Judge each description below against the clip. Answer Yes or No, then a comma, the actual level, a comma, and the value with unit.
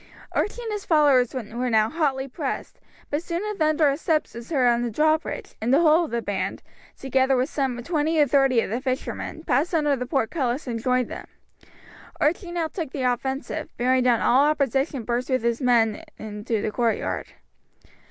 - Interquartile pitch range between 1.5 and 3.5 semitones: No, average, 4.1 semitones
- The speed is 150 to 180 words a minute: No, average, 190 wpm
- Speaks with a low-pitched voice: No, very high, 265 Hz